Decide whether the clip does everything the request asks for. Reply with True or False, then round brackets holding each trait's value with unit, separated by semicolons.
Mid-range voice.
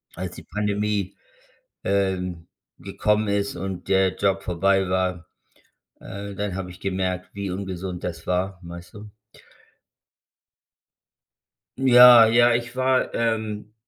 False (95 Hz)